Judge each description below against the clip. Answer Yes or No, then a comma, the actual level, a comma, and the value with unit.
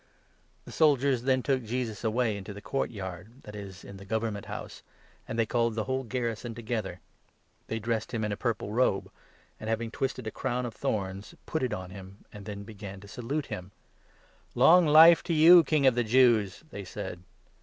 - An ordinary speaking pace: No, fast, 215 wpm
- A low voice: Yes, low, 115 Hz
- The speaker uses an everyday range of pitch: Yes, average, 4.1 semitones